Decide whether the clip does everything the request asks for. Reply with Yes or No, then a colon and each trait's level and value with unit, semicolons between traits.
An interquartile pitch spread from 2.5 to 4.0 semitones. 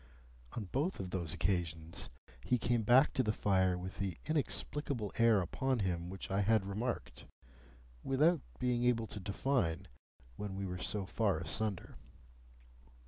No: average, 4.8 semitones